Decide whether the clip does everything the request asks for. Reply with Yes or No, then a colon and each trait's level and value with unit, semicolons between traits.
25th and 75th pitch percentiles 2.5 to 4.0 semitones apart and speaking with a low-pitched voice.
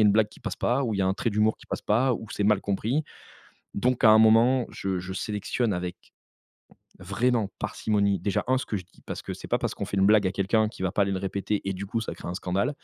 Yes: average, 2.8 semitones; low, 105 Hz